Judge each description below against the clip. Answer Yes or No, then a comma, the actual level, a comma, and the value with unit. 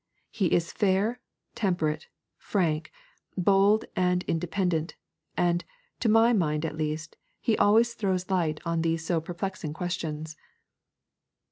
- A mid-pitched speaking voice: Yes, medium, 175 Hz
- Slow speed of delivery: Yes, slow, 120 wpm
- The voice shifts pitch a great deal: No, average, 3.5 semitones